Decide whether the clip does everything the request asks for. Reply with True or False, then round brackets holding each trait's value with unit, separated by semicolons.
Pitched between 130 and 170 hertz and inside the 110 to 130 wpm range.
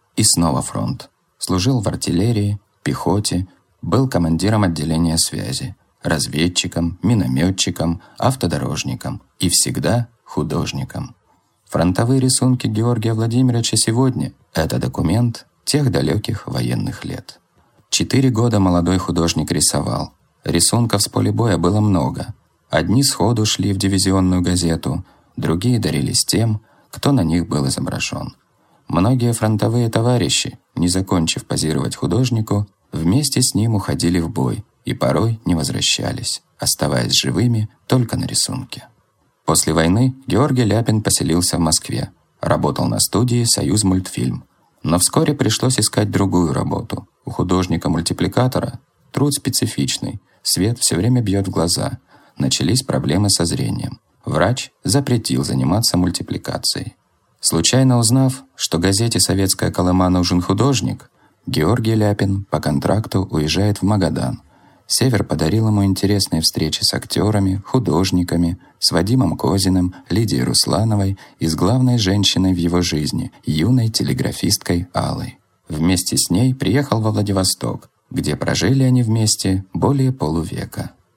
False (100 Hz; 120 wpm)